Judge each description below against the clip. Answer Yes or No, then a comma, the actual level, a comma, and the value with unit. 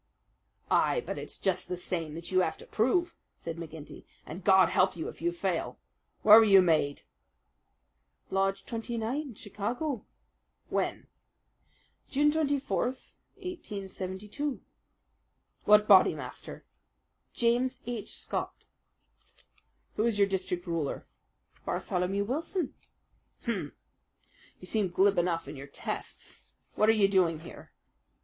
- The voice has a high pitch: Yes, high, 195 Hz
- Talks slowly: Yes, slow, 120 wpm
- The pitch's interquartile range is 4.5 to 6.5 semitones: Yes, average, 5.0 semitones